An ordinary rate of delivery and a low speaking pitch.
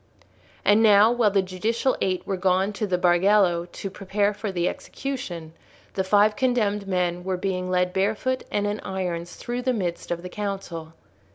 No: average, 175 wpm; high, 195 Hz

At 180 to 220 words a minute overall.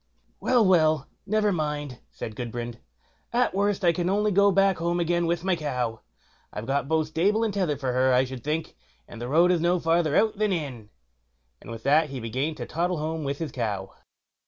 Yes: fast, 205 wpm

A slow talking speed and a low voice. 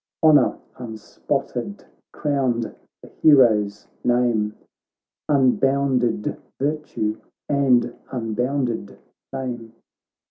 Yes: slow, 65 wpm; low, 125 Hz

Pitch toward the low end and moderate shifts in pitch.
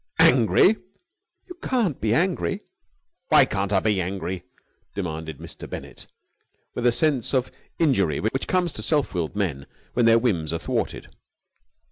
No: low, 110 Hz; wide, 7.4 semitones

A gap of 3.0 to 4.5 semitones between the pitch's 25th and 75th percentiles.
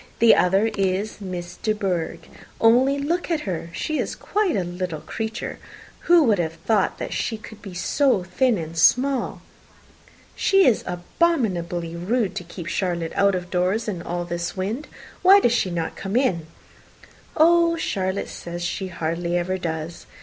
No: wide, 5.6 semitones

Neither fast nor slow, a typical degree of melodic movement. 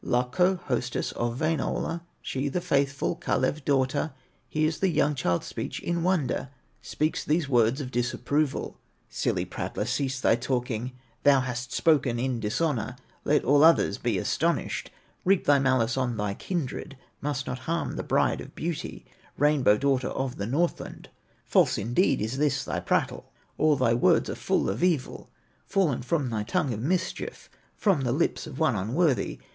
Yes: average, 160 wpm; average, 4.2 semitones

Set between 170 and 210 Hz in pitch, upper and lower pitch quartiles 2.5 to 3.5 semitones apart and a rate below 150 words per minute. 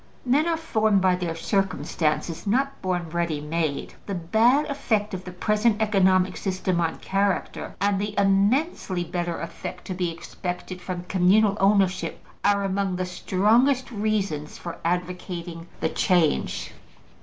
Yes: high, 190 Hz; average, 3.0 semitones; average, 140 wpm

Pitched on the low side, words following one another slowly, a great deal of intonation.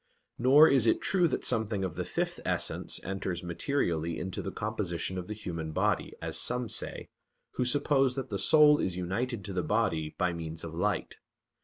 No: low, 100 Hz; average, 185 wpm; wide, 6.3 semitones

